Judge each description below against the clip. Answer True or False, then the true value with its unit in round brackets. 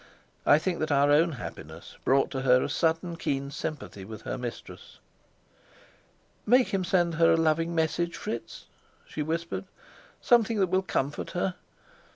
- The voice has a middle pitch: True (165 Hz)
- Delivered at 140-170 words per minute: True (155 wpm)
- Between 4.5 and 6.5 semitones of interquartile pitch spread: False (3.7 semitones)